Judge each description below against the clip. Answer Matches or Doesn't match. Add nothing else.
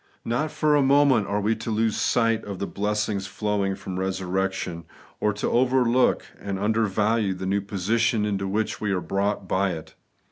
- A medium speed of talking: Matches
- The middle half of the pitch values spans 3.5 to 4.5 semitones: Doesn't match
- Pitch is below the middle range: Matches